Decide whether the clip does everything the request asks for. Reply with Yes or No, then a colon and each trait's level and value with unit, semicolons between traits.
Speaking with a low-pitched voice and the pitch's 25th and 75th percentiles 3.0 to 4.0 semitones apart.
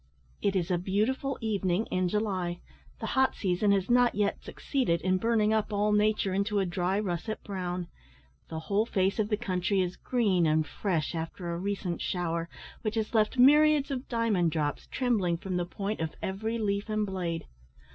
No: high, 200 Hz; average, 3.5 semitones